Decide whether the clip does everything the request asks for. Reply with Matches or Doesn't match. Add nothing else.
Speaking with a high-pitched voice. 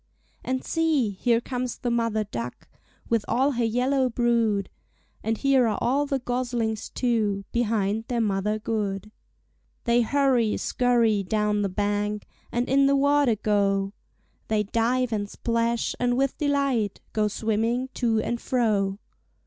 Matches